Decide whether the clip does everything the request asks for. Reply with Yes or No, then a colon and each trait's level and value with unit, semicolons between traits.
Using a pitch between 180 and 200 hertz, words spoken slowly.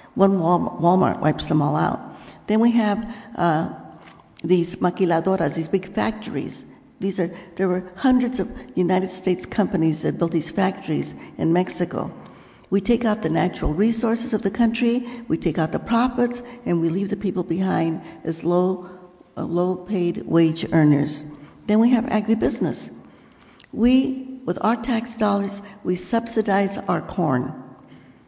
No: high, 190 Hz; average, 150 wpm